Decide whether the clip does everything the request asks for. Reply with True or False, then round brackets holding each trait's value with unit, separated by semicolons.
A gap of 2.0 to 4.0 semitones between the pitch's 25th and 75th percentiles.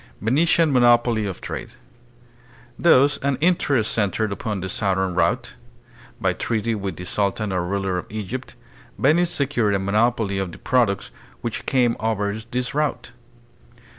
False (4.5 semitones)